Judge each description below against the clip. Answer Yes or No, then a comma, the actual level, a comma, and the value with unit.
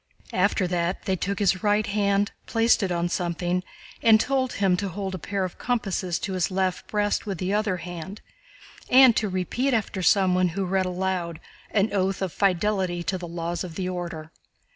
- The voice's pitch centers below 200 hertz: Yes, high, 190 Hz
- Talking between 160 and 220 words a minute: Yes, average, 185 wpm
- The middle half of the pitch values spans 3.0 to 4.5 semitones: No, narrow, 2.4 semitones